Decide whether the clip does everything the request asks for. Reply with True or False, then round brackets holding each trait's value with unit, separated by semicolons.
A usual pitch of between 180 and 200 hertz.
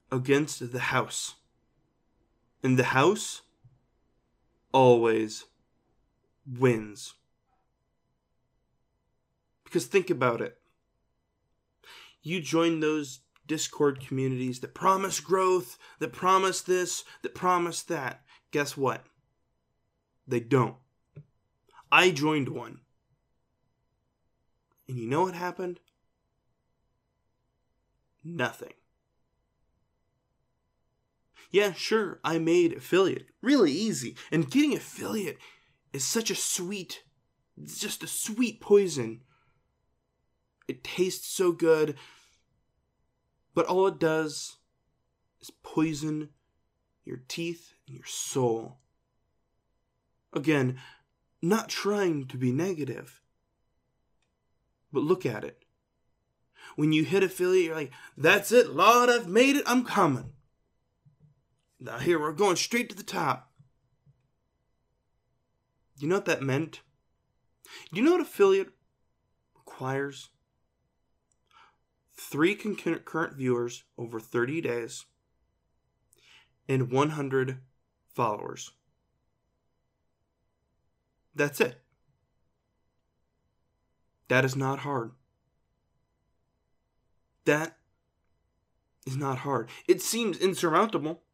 False (140 Hz)